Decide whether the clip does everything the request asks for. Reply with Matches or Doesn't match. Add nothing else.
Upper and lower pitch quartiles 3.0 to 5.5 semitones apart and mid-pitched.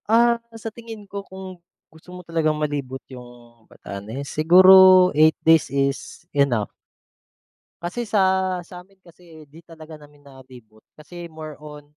Matches